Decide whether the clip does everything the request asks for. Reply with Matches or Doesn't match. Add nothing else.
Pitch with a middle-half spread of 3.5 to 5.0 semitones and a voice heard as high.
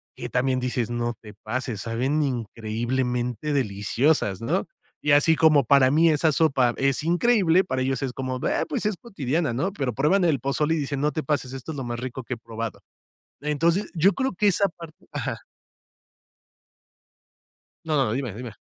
Doesn't match